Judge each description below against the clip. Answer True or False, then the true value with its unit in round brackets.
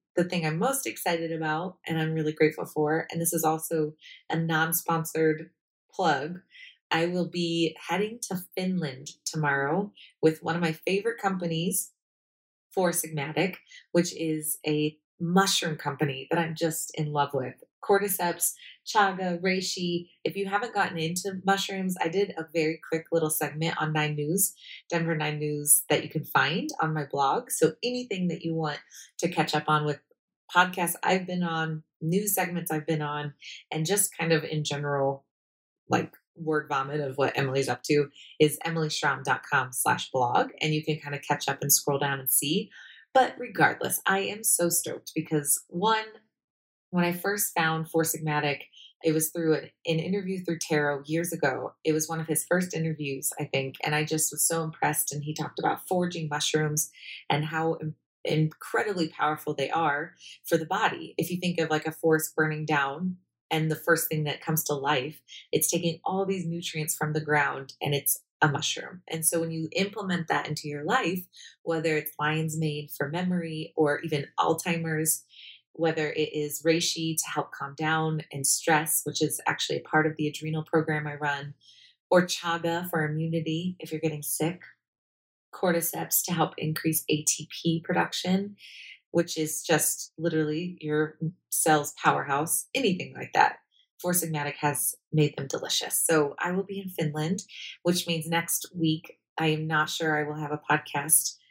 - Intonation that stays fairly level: True (2.2 semitones)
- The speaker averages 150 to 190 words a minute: True (175 wpm)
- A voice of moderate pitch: True (160 Hz)